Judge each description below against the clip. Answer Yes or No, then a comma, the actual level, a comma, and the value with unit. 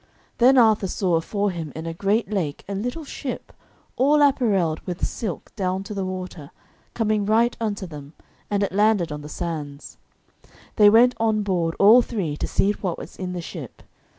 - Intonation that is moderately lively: Yes, average, 4.4 semitones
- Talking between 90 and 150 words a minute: No, average, 180 wpm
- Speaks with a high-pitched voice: Yes, high, 200 Hz